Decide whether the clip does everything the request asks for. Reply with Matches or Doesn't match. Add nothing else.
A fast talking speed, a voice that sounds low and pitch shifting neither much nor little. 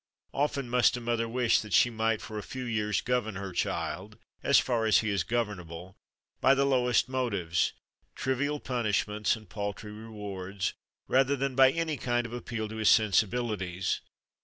Doesn't match